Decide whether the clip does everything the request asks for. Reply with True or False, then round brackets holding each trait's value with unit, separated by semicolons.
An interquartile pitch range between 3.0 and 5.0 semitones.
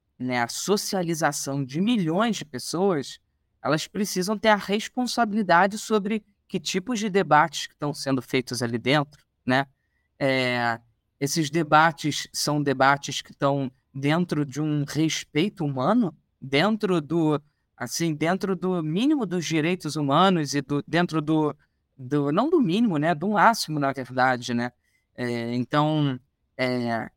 False (5.6 semitones)